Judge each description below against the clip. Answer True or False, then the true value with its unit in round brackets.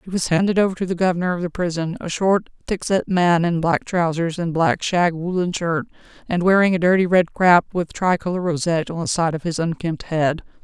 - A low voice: False (175 Hz)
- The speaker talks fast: True (220 wpm)